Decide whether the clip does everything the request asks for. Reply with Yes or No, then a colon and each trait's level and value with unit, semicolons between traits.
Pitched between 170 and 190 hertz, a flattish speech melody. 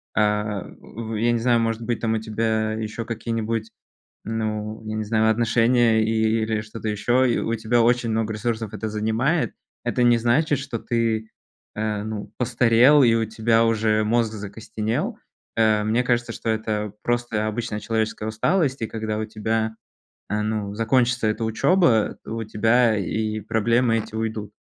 No: low, 110 Hz; narrow, 1.4 semitones